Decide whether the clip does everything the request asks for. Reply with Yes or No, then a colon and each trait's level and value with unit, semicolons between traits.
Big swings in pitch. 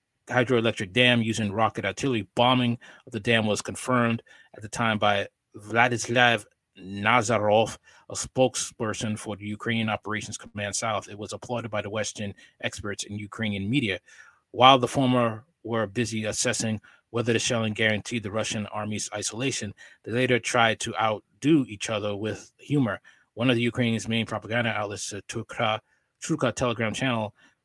No: narrow, 2.5 semitones